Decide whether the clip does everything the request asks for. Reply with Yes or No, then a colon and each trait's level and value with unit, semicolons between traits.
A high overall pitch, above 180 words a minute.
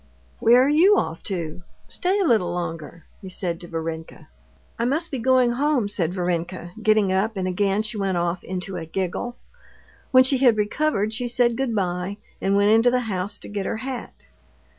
Yes: high, 205 Hz; average, 190 wpm